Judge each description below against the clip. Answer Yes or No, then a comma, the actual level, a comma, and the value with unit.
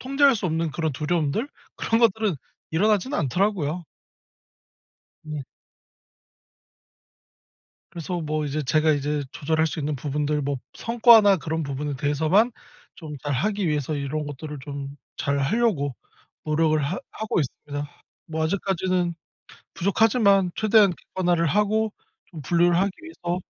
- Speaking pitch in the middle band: Yes, medium, 160 Hz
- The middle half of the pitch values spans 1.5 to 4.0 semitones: No, average, 5.2 semitones